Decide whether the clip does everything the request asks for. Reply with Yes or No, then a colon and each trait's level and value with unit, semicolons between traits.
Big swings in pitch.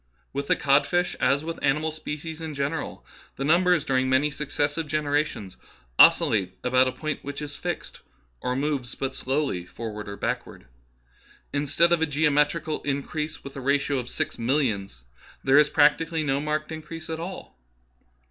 No: narrow, 2.6 semitones